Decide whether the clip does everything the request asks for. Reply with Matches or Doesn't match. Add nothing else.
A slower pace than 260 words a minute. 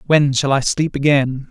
Matches